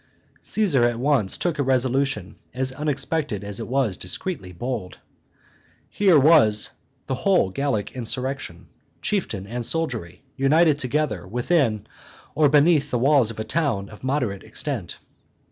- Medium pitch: No, low, 130 Hz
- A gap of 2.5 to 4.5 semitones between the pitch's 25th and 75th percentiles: No, wide, 5.4 semitones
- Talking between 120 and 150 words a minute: Yes, slow, 135 wpm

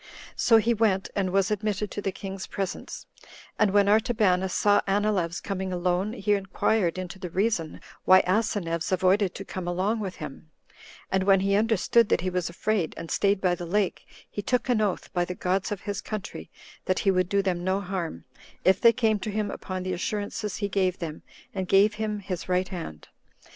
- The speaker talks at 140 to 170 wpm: No, average, 195 wpm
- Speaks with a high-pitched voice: Yes, high, 195 Hz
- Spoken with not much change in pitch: Yes, narrow, 2.3 semitones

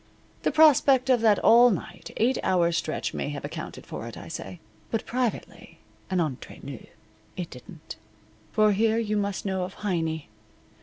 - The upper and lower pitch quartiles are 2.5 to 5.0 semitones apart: No, wide, 5.4 semitones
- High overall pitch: Yes, high, 200 Hz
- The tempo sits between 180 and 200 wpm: No, average, 165 wpm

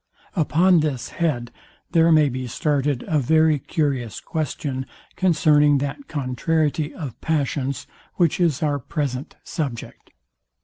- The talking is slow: Yes, slow, 120 wpm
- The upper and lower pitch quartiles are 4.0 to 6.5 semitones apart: No, average, 3.2 semitones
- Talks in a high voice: No, medium, 150 Hz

